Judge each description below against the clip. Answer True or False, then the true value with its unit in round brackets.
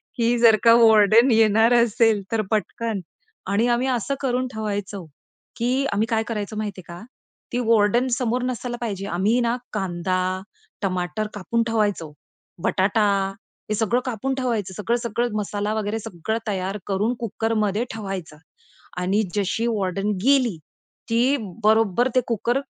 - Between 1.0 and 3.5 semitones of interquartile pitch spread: True (2.8 semitones)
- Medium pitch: False (220 Hz)